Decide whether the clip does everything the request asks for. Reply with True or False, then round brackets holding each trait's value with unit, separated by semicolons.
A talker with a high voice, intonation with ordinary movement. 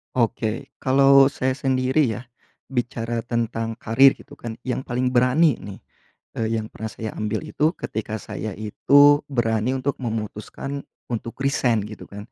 False (120 Hz; 3.2 semitones)